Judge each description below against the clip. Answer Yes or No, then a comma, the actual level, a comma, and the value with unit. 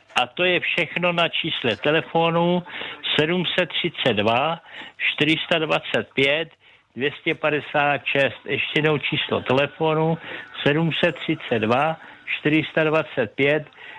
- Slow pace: Yes, slow, 70 wpm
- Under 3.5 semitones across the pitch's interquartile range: Yes, narrow, 2.4 semitones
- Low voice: No, medium, 155 Hz